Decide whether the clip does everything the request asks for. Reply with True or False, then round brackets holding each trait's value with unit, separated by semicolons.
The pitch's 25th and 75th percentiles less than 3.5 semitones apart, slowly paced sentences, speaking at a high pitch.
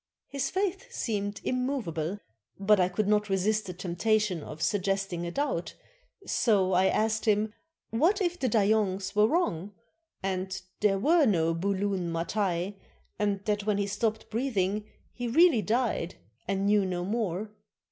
False (2.8 semitones; 150 wpm; 205 Hz)